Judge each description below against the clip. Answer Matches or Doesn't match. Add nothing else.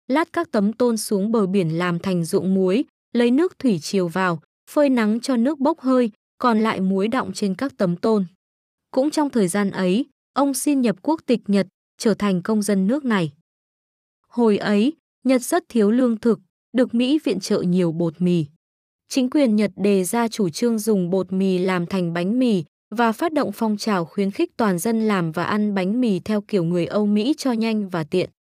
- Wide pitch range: Doesn't match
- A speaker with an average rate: Matches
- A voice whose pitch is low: Doesn't match